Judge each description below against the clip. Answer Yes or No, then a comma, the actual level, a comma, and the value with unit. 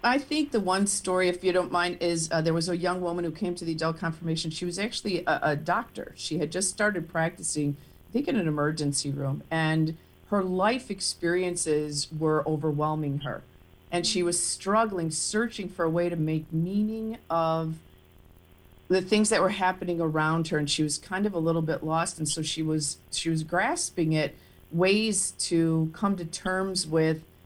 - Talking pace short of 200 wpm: Yes, average, 190 wpm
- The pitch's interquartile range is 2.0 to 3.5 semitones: Yes, average, 2.9 semitones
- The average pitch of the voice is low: No, medium, 165 Hz